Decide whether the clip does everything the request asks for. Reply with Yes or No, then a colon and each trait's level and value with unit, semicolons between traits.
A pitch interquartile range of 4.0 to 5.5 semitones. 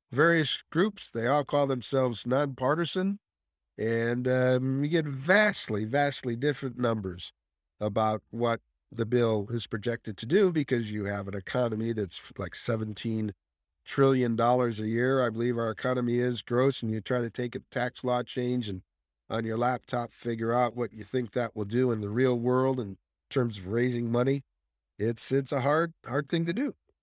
No: average, 3.2 semitones